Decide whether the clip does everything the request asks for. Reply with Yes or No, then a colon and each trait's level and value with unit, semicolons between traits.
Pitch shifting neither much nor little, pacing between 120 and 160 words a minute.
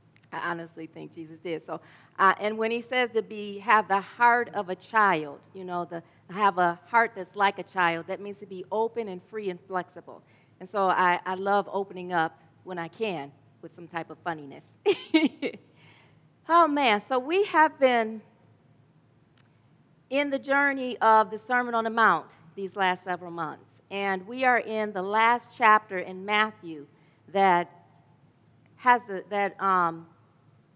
No: average, 5.0 semitones; average, 170 wpm